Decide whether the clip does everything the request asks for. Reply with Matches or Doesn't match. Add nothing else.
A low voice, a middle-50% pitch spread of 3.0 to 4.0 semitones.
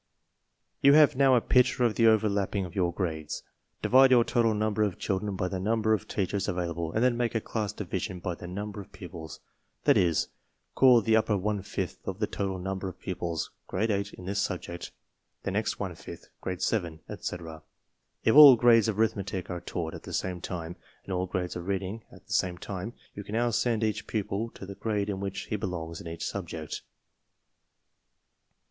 Matches